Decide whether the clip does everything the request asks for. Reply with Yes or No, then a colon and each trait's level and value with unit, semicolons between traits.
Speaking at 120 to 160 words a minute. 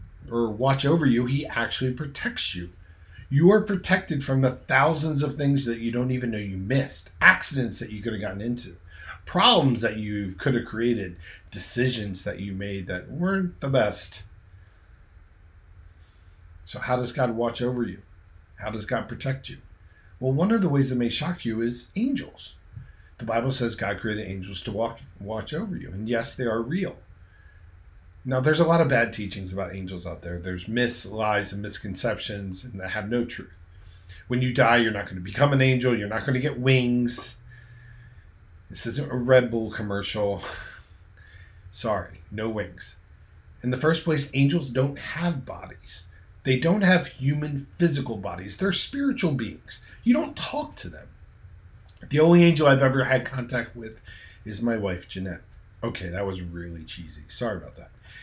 No: average, 175 wpm